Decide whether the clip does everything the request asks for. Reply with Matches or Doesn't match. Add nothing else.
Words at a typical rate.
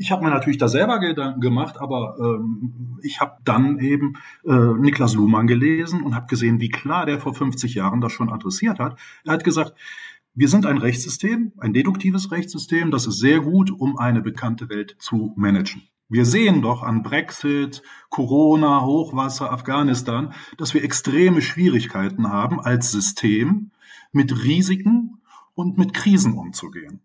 Matches